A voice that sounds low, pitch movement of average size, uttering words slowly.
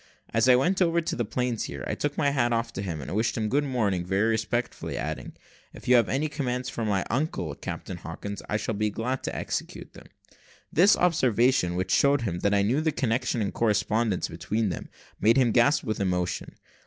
No: low, 115 Hz; average, 4.7 semitones; fast, 205 wpm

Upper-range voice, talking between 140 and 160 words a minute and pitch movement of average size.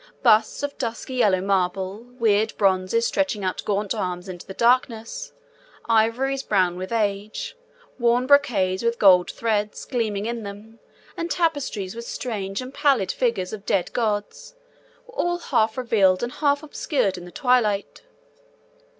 Yes: high, 220 Hz; average, 145 wpm; average, 4.2 semitones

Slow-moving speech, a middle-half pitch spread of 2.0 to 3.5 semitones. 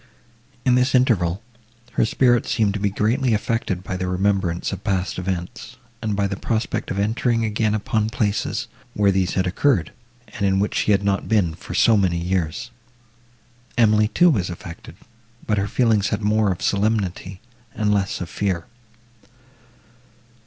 No: average, 160 wpm; average, 3.0 semitones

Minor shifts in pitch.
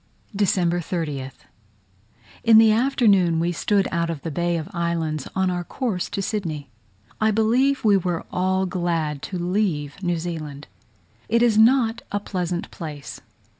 No: average, 4.1 semitones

